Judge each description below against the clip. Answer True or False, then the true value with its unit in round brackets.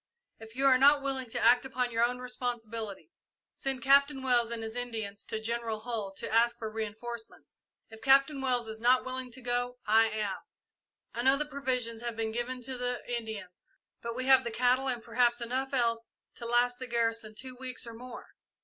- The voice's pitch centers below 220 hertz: False (240 Hz)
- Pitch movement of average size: False (2.2 semitones)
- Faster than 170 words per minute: True (195 wpm)